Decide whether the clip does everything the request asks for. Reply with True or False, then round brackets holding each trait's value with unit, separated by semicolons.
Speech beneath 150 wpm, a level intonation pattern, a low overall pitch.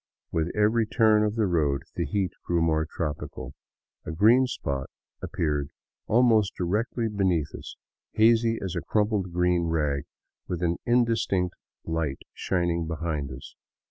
False (140 wpm; 5.1 semitones; 90 Hz)